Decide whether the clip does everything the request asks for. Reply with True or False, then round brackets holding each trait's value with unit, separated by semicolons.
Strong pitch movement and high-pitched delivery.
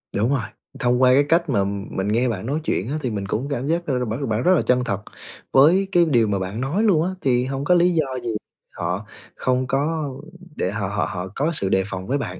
False (6.1 semitones; 125 Hz)